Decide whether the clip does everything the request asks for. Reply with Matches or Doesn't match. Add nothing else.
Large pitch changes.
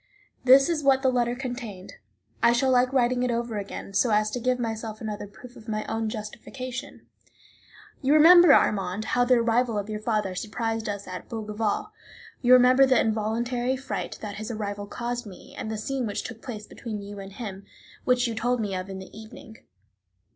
Doesn't match